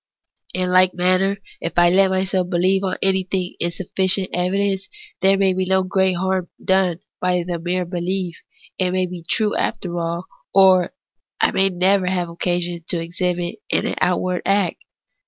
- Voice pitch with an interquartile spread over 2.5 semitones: No, narrow, 1.3 semitones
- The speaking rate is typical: Yes, average, 160 wpm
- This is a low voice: No, medium, 185 Hz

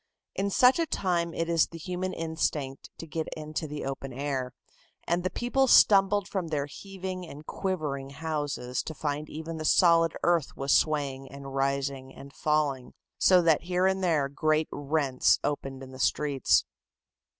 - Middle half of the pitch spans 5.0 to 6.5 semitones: No, average, 4.0 semitones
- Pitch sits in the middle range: Yes, medium, 155 Hz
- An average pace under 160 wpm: No, average, 165 wpm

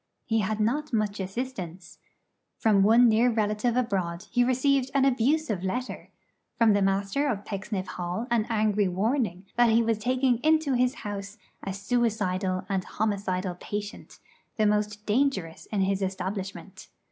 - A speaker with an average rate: Yes, average, 145 wpm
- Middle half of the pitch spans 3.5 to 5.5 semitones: Yes, average, 3.9 semitones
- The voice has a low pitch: No, high, 210 Hz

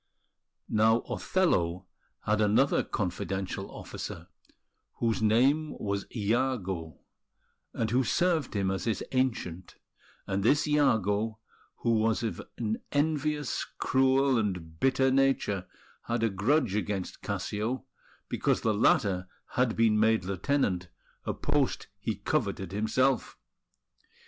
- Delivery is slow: Yes, slow, 115 wpm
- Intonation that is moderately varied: Yes, average, 4.9 semitones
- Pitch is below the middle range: Yes, low, 110 Hz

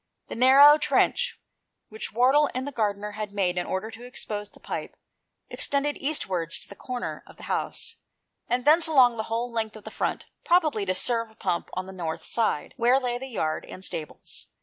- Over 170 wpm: Yes, average, 195 wpm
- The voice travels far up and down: No, average, 4.7 semitones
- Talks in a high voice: Yes, high, 230 Hz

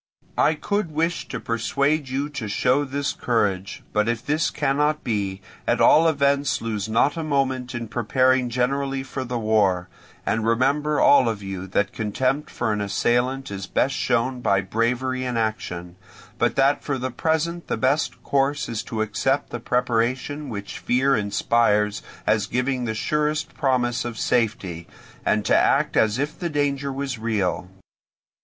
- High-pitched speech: No, low, 125 Hz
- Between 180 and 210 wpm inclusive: No, average, 160 wpm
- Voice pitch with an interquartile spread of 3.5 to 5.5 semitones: Yes, average, 4.2 semitones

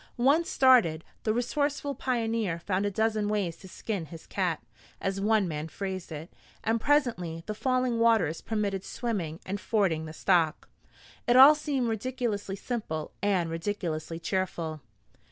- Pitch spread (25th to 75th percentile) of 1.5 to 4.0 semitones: No, wide, 5.6 semitones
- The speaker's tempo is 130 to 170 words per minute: Yes, average, 145 wpm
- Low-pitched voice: No, high, 205 Hz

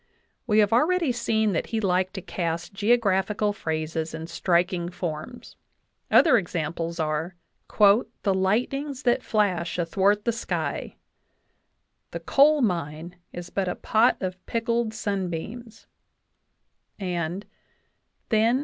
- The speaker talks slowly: Yes, slow, 115 wpm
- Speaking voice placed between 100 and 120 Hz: No, high, 195 Hz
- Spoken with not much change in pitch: No, average, 4.8 semitones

